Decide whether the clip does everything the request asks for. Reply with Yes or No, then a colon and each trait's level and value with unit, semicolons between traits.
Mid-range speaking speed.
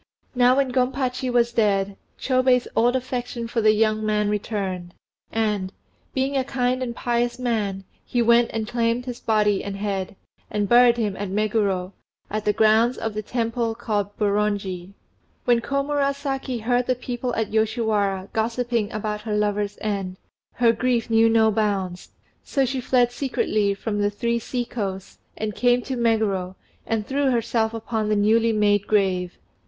Yes: average, 160 wpm